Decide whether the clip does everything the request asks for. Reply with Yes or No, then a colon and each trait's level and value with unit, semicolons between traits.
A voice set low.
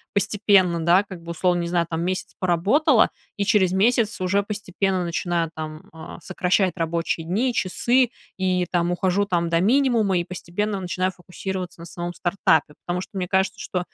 No: medium, 185 Hz